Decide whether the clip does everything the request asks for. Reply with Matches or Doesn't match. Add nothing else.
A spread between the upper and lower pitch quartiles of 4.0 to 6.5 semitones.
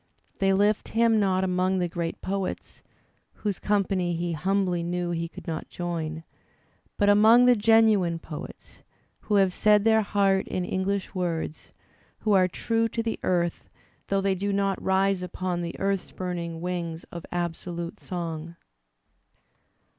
Doesn't match